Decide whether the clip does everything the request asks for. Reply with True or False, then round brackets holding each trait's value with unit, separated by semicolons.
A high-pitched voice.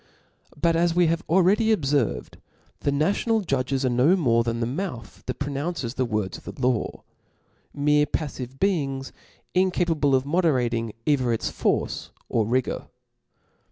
False (140 Hz)